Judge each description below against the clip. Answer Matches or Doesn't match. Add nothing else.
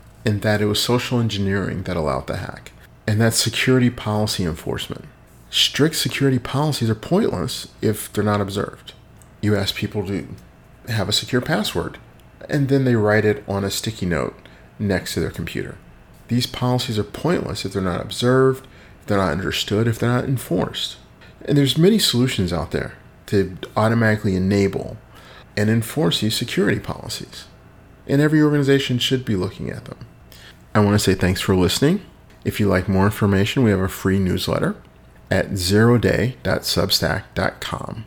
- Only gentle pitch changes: Doesn't match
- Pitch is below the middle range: Matches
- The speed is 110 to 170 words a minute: Matches